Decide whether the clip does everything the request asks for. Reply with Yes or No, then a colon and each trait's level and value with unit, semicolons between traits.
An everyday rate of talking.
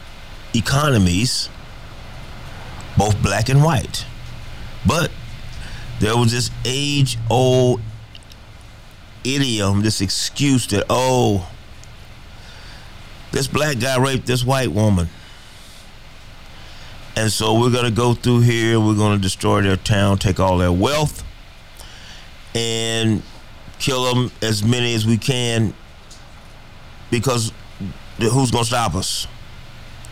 No: slow, 110 wpm